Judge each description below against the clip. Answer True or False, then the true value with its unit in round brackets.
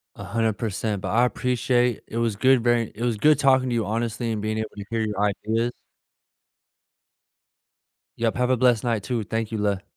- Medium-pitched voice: False (115 Hz)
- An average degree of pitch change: False (2.1 semitones)